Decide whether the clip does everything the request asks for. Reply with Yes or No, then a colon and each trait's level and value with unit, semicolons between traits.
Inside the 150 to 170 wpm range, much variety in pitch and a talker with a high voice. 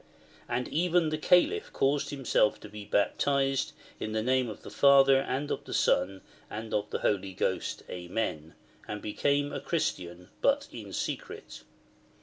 No: average, 155 wpm; wide, 5.7 semitones; low, 125 Hz